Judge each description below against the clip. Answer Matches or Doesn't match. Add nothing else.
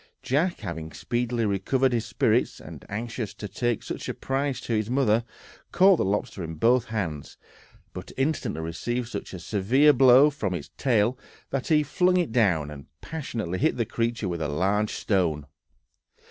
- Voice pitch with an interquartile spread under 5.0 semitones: Doesn't match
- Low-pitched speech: Matches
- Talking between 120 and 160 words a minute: Doesn't match